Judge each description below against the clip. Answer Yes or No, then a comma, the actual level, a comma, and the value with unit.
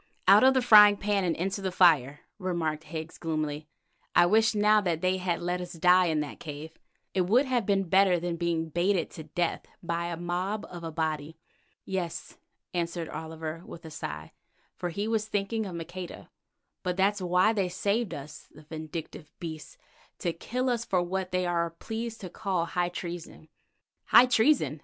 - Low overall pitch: No, medium, 175 Hz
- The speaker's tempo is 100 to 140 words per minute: No, average, 175 wpm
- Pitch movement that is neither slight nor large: Yes, average, 3.3 semitones